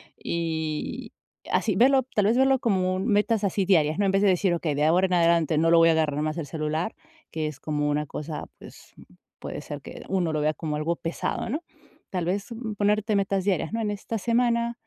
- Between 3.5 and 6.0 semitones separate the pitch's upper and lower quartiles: Yes, average, 4.7 semitones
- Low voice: No, medium, 180 Hz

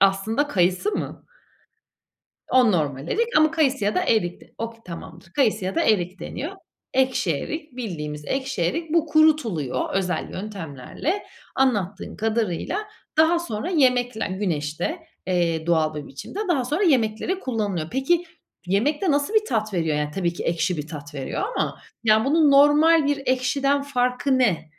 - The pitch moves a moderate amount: No, wide, 8.7 semitones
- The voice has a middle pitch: No, high, 225 Hz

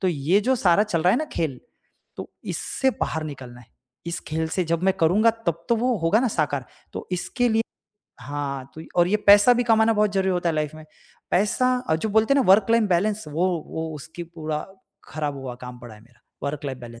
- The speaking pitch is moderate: Yes, medium, 170 Hz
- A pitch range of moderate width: No, wide, 6.4 semitones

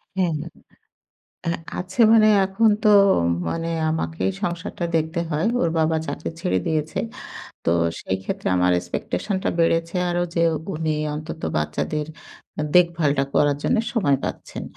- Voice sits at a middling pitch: Yes, medium, 160 Hz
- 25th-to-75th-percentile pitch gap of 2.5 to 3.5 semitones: Yes, average, 2.9 semitones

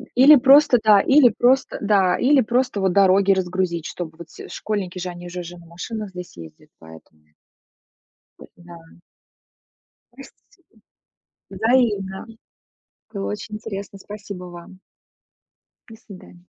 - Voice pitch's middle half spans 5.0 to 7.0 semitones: No, average, 3.8 semitones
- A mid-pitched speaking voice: No, high, 195 Hz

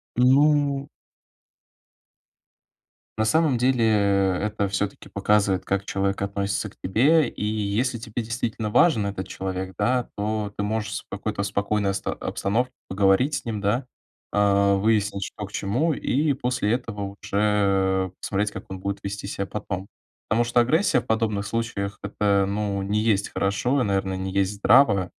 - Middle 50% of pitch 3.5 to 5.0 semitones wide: No, average, 2.9 semitones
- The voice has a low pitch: Yes, low, 105 Hz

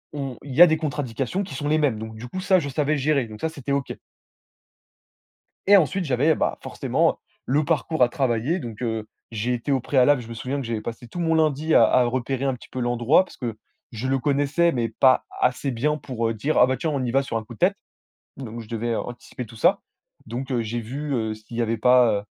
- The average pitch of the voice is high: No, low, 130 Hz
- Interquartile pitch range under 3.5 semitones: No, average, 3.8 semitones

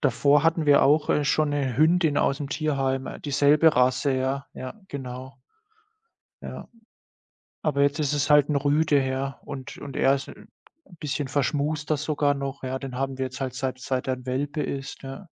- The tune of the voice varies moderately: No, narrow, 1.9 semitones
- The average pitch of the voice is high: No, medium, 140 Hz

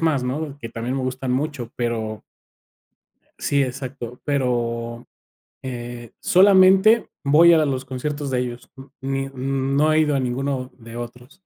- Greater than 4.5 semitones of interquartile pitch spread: No, average, 2.9 semitones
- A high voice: No, low, 130 Hz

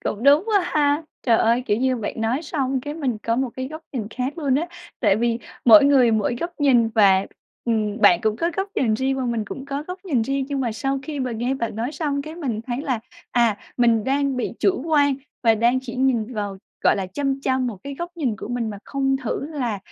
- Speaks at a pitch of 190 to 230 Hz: No, very high, 255 Hz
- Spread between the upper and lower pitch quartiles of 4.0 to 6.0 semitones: No, average, 3.6 semitones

